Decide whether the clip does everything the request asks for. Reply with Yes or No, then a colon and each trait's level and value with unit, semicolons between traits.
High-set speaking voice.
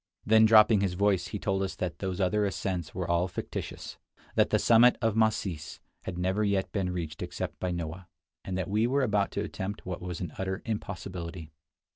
No: very low, 95 Hz